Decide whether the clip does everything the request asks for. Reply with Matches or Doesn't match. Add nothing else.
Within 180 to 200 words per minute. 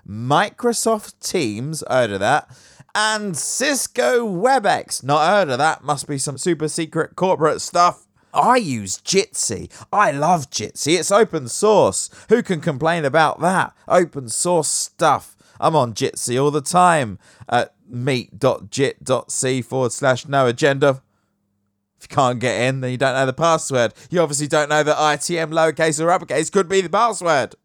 Doesn't match